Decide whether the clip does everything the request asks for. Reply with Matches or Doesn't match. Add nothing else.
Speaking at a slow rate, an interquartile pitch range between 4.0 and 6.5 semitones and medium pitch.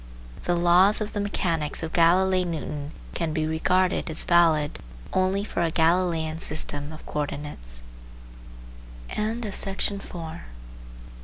Doesn't match